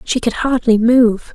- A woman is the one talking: Yes, female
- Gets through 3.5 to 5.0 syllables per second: Yes, 4.0 syllables/s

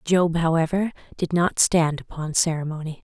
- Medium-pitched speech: Yes, medium, 165 Hz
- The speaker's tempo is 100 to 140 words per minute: Yes, slow, 135 wpm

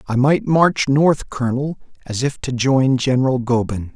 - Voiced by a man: Yes, male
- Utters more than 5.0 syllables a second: No, 4.5 syllables/s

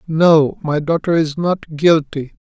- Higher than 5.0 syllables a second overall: No, 3.7 syllables/s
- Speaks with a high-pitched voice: No, medium, 155 Hz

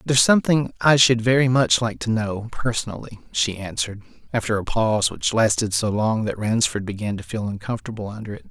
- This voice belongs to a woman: No, male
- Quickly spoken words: No, average, 185 wpm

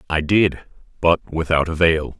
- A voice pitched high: No, very low, 80 Hz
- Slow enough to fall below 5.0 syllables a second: Yes, 4.2 syllables/s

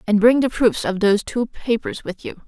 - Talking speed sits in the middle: No, fast, 245 wpm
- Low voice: No, high, 225 Hz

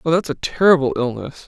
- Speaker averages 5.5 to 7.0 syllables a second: Yes, 6.0 syllables/s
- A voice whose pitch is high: No, medium, 145 Hz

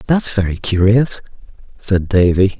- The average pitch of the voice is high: No, low, 100 Hz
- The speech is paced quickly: No, slow, 115 wpm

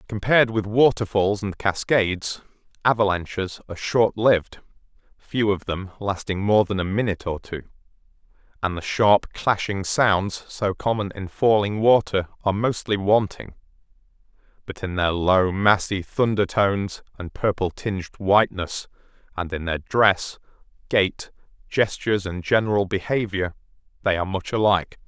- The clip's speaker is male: Yes, male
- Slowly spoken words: Yes, slow, 130 wpm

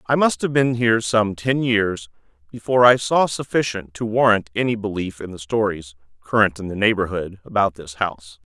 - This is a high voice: No, low, 105 Hz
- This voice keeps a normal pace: Yes, average, 185 wpm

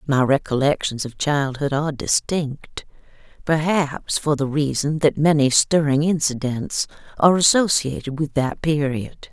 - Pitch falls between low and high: Yes, medium, 145 Hz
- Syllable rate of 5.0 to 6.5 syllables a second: No, 4.4 syllables/s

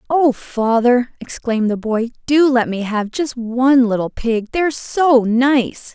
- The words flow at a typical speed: Yes, average, 170 wpm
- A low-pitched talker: No, high, 245 Hz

